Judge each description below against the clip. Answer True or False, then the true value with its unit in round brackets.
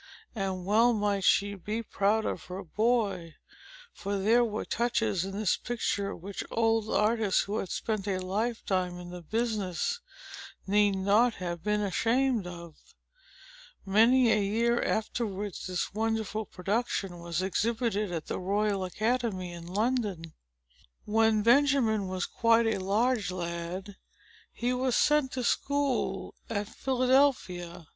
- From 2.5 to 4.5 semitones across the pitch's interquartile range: True (3.7 semitones)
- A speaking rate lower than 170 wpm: True (135 wpm)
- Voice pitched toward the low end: False (210 Hz)